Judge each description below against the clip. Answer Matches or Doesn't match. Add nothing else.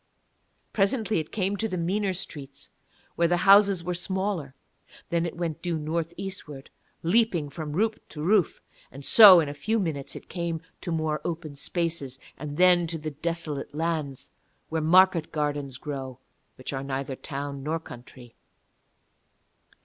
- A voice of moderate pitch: Matches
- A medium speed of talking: Matches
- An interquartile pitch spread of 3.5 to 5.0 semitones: Matches